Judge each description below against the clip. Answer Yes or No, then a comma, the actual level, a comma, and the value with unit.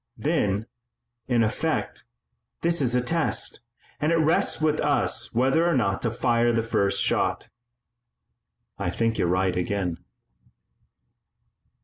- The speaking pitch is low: Yes, low, 115 Hz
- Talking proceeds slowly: Yes, slow, 125 wpm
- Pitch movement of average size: No, wide, 7.0 semitones